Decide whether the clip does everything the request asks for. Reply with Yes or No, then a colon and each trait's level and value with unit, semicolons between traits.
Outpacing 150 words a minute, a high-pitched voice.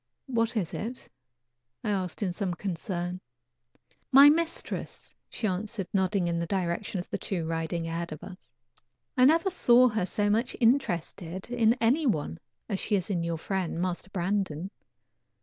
Yes: average, 160 wpm; high, 195 Hz